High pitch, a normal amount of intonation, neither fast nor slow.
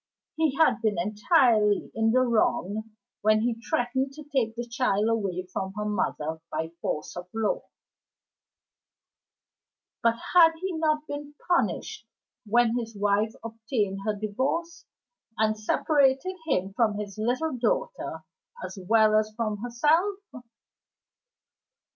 No: high, 225 Hz; average, 4.3 semitones; slow, 125 wpm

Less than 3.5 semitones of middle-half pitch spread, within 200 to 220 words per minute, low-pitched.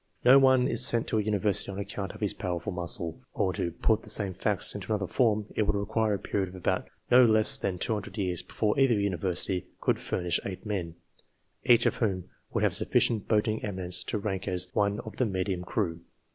Yes: average, 2.9 semitones; fast, 205 wpm; low, 100 Hz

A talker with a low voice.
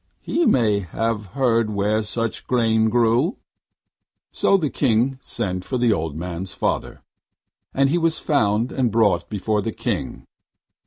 Yes: low, 115 Hz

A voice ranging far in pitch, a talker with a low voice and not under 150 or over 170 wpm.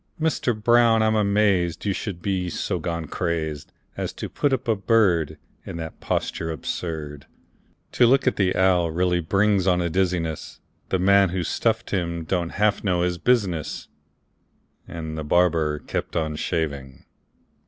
No: average, 3.6 semitones; very low, 90 Hz; average, 155 wpm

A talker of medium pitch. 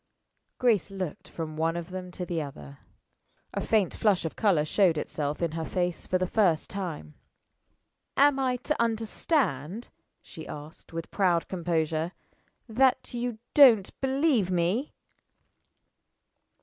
Yes: medium, 180 Hz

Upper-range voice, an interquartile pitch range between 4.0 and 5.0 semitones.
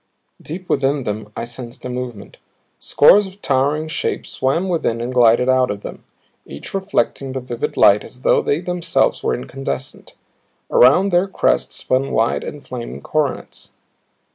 No: low, 130 Hz; average, 4.6 semitones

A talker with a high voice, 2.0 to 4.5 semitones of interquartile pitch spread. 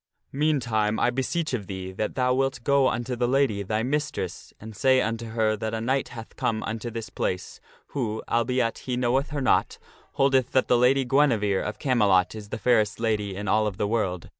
No: low, 115 Hz; average, 3.4 semitones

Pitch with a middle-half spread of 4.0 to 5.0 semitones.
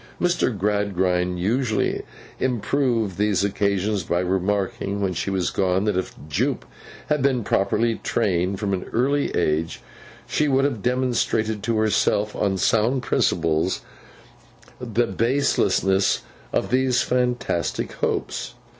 Yes: average, 4.5 semitones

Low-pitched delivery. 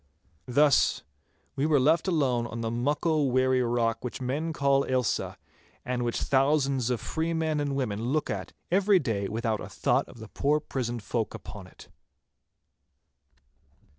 Yes: low, 130 Hz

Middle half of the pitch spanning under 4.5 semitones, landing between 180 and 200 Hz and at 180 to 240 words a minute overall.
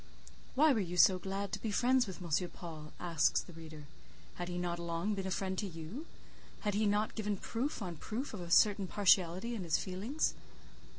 Yes: average, 3.7 semitones; high, 190 Hz; average, 200 wpm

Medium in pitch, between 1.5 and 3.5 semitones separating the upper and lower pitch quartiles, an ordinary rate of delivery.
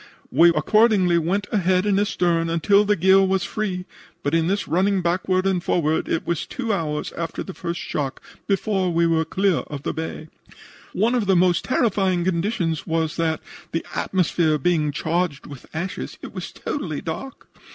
Yes: medium, 175 Hz; average, 3.0 semitones; average, 170 wpm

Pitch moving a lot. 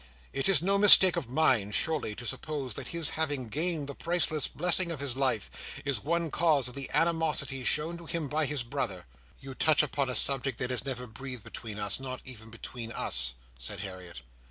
No: average, 4.9 semitones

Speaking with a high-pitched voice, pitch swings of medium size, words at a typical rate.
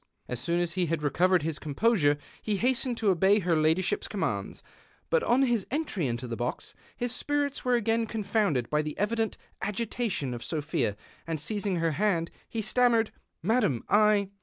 No: high, 195 Hz; wide, 6.5 semitones; average, 180 wpm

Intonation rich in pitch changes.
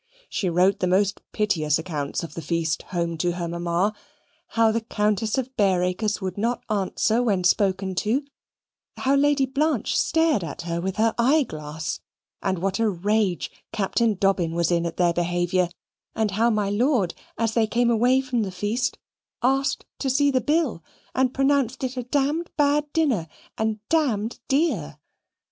Yes: wide, 6.3 semitones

